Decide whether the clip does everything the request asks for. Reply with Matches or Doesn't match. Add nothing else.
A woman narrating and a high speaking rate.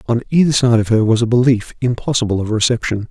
Doesn't match